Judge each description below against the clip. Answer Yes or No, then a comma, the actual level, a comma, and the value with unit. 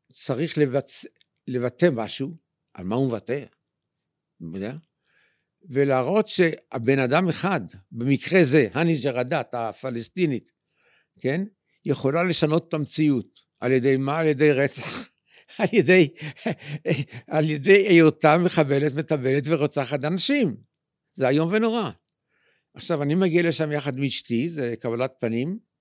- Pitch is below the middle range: No, medium, 150 Hz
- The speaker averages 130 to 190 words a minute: No, average, 115 wpm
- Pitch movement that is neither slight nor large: Yes, average, 3.9 semitones